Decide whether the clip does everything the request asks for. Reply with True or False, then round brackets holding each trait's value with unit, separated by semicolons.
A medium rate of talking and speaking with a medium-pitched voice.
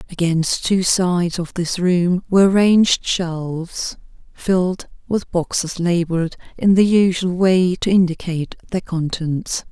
False (130 wpm; 180 Hz)